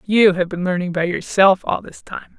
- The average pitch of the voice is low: No, medium, 185 Hz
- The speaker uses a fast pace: Yes, fast, 225 wpm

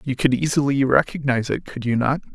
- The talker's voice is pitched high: No, low, 130 Hz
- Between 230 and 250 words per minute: No, fast, 205 wpm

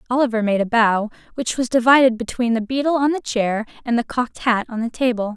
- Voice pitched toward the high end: Yes, high, 240 Hz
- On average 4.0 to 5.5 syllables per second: No, 5.9 syllables/s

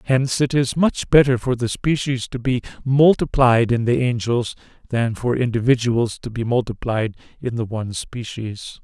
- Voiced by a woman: No, male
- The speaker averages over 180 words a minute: No, average, 165 wpm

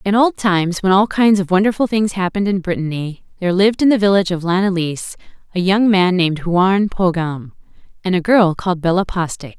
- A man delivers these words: No, female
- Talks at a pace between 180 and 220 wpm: Yes, average, 195 wpm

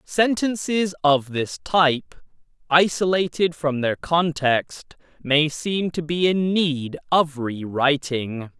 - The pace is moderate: No, slow, 110 wpm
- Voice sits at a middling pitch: Yes, medium, 150 Hz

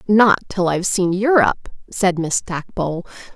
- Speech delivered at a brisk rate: No, average, 145 wpm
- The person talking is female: Yes, female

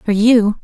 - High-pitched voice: Yes, high, 220 Hz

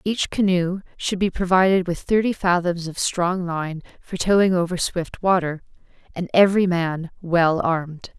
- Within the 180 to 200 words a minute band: No, average, 155 wpm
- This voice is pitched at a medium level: Yes, medium, 180 Hz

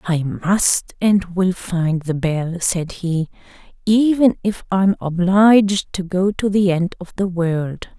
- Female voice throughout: Yes, female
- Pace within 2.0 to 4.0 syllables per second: Yes, 3.6 syllables/s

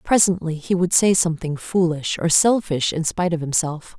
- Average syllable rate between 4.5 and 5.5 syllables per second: Yes, 5.2 syllables/s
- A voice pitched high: No, medium, 170 Hz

